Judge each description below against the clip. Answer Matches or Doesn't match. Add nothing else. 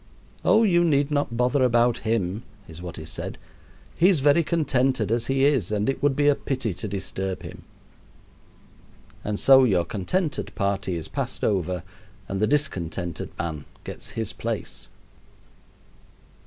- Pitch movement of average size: Doesn't match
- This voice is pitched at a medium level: Doesn't match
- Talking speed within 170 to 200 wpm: Doesn't match